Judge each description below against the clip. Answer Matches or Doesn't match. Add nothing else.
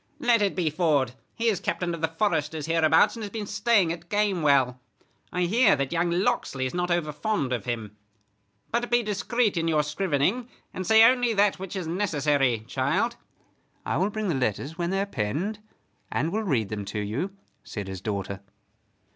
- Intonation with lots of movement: Matches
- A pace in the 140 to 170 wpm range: Doesn't match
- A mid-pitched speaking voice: Matches